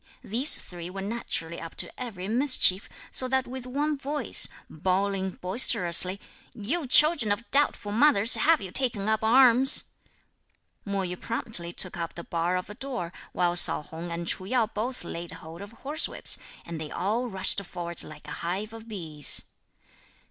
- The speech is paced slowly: No, average, 165 wpm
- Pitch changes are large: Yes, wide, 6.1 semitones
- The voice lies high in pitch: Yes, high, 200 Hz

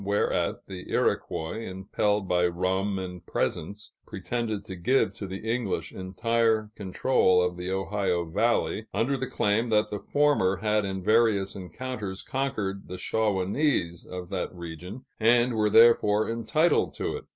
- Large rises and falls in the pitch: No, average, 3.7 semitones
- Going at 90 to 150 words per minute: Yes, average, 145 wpm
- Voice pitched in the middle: No, low, 100 Hz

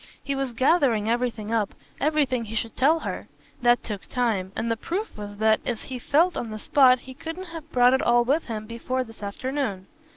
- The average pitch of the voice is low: No, high, 245 Hz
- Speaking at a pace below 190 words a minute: No, fast, 205 wpm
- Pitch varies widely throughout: No, average, 3.9 semitones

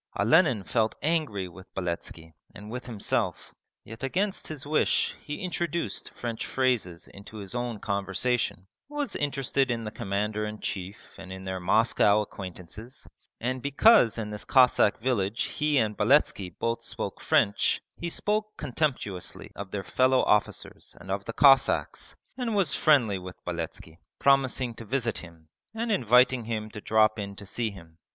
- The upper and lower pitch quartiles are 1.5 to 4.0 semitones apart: No, average, 5.3 semitones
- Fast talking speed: No, average, 155 wpm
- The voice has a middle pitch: No, low, 115 Hz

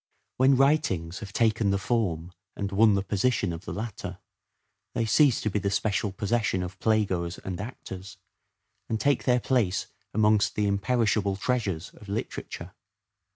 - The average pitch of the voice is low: Yes, low, 105 Hz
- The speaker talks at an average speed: Yes, average, 155 wpm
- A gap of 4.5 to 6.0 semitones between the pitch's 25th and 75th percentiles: No, average, 3.1 semitones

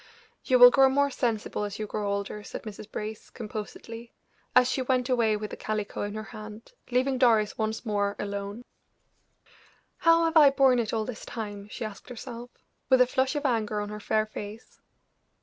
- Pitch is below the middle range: No, high, 220 Hz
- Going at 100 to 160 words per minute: No, average, 185 wpm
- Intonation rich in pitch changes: No, average, 3.1 semitones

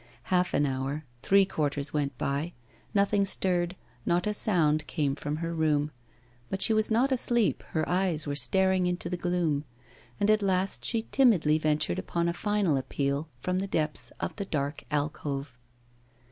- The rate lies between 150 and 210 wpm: Yes, average, 165 wpm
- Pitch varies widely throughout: No, average, 4.6 semitones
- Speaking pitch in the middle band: Yes, medium, 170 Hz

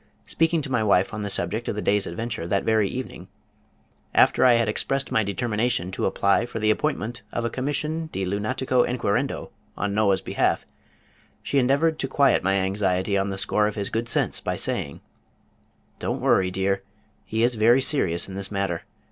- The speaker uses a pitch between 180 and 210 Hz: No, low, 110 Hz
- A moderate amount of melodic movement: Yes, average, 4.2 semitones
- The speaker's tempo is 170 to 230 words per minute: Yes, average, 185 wpm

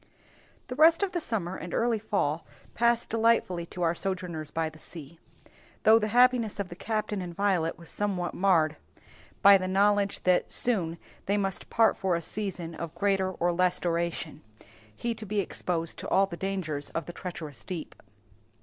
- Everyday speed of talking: Yes, average, 175 wpm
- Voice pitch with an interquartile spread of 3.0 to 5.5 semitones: Yes, average, 3.7 semitones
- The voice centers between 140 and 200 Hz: Yes, medium, 185 Hz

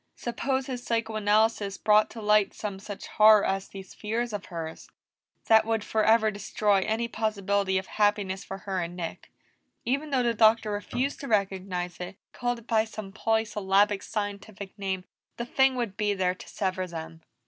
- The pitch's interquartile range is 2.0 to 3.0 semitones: Yes, narrow, 2.5 semitones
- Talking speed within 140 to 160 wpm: No, average, 170 wpm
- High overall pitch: Yes, high, 210 Hz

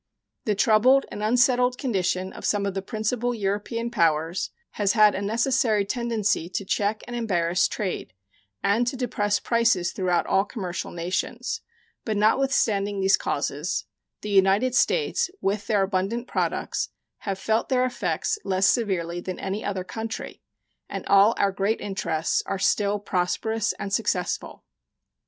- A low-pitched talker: No, high, 205 Hz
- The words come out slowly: No, average, 145 wpm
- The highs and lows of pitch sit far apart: No, average, 3.2 semitones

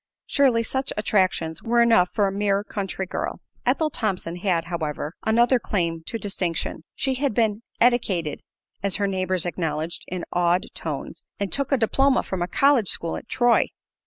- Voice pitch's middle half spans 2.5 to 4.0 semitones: No, average, 5.0 semitones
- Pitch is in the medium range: No, high, 200 Hz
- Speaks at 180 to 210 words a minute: No, average, 165 wpm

